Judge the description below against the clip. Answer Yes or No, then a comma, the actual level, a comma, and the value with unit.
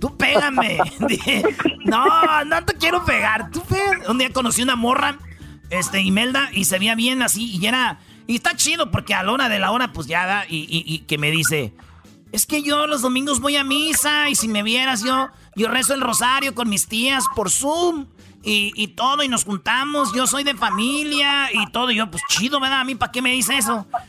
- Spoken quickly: Yes, fast, 220 wpm